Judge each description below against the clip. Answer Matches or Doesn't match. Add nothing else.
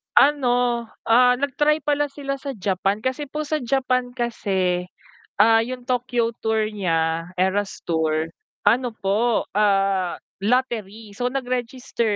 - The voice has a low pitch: Doesn't match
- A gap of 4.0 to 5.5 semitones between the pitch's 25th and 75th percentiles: Matches